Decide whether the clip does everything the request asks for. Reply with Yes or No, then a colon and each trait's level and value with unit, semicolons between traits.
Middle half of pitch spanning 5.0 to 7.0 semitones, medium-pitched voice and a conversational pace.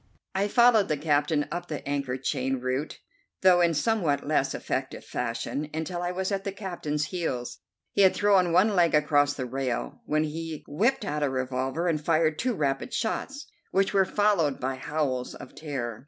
Yes: average, 5.3 semitones; medium, 155 Hz; average, 180 wpm